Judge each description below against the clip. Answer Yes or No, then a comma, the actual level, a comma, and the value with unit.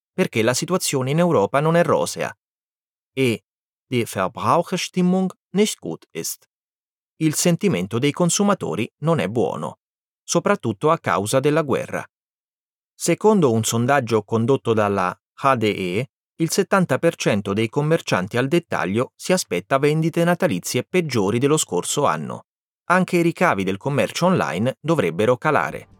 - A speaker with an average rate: Yes, average, 125 wpm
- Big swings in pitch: Yes, wide, 7.3 semitones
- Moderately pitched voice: Yes, medium, 150 Hz